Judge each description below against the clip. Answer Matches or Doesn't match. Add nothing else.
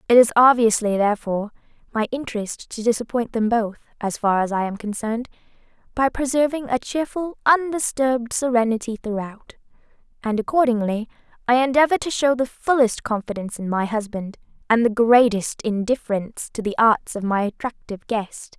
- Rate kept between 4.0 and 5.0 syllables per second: Doesn't match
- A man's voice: Doesn't match